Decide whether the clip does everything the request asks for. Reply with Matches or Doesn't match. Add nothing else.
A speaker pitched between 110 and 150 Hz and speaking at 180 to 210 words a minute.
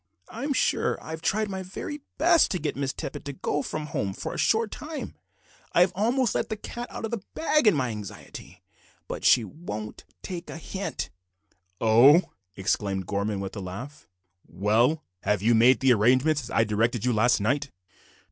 Matches